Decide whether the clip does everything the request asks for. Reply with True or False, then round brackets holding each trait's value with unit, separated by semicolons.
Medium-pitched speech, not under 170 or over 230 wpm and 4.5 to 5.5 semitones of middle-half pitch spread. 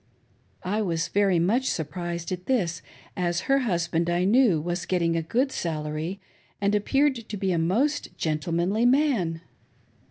False (180 Hz; 155 wpm; 5.1 semitones)